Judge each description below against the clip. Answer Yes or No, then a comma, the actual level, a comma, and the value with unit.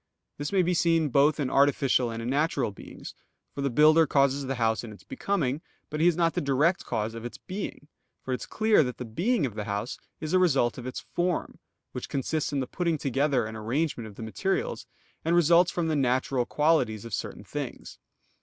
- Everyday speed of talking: No, fast, 220 wpm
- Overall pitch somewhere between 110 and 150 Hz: Yes, medium, 140 Hz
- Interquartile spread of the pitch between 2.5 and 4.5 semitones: No, average, 5.2 semitones